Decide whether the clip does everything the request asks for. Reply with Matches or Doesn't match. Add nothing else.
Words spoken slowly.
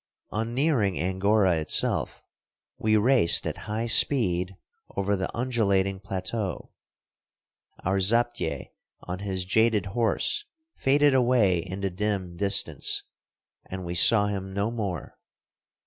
Matches